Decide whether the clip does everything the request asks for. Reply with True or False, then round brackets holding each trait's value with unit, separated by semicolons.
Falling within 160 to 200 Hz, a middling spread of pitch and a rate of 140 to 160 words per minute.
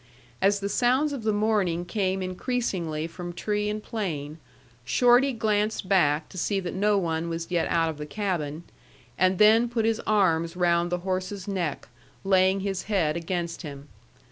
False (185 Hz; 3.9 semitones; 170 wpm)